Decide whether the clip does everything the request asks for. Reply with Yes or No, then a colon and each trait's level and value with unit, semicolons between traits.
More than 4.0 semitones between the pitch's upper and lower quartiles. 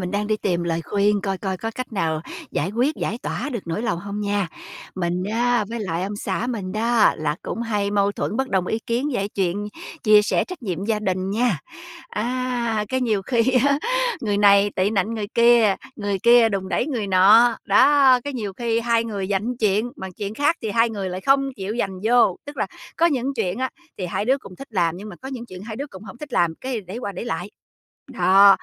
No: average, 3.7 semitones